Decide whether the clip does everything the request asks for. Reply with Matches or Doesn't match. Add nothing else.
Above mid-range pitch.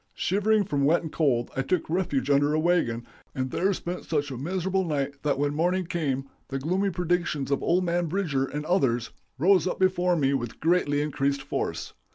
Doesn't match